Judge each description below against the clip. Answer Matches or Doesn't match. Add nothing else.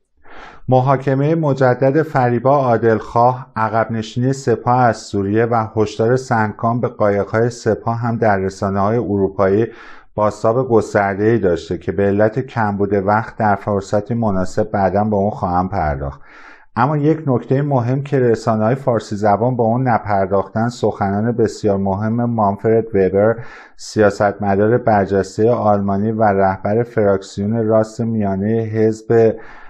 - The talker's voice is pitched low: Matches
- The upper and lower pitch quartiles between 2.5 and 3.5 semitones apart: Matches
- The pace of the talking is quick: Doesn't match